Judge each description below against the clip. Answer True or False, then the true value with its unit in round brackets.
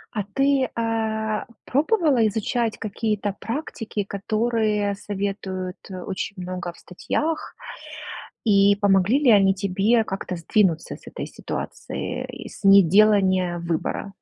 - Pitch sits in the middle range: False (205 Hz)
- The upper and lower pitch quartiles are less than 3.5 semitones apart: True (2.8 semitones)